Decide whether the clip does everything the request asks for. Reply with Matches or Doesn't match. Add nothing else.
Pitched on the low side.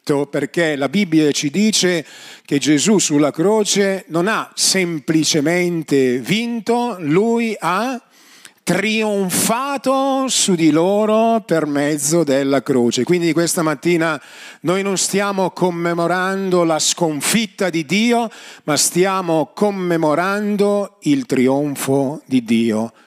Doesn't match